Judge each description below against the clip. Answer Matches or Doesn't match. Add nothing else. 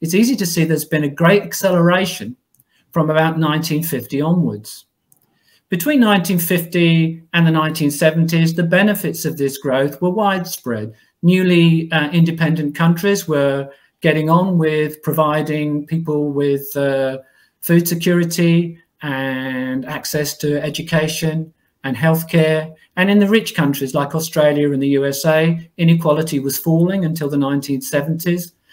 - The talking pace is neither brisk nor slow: Doesn't match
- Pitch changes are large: Doesn't match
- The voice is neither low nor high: Matches